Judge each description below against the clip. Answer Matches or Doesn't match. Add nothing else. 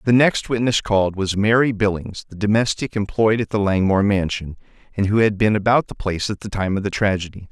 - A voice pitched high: Doesn't match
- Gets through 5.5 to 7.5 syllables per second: Matches